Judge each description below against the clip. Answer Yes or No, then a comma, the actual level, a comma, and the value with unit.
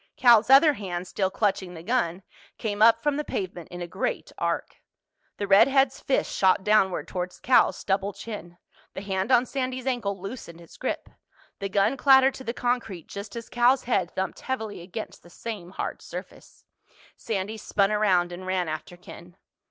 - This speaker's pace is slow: No, average, 175 wpm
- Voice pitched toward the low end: No, high, 200 Hz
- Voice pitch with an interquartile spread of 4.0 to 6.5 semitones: Yes, average, 4.8 semitones